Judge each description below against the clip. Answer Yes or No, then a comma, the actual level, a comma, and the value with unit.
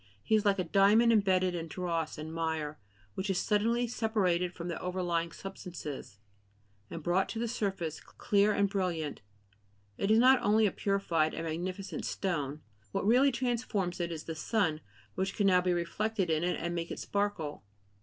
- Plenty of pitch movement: No, average, 3.7 semitones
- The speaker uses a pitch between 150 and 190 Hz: Yes, medium, 185 Hz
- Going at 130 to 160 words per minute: No, average, 175 wpm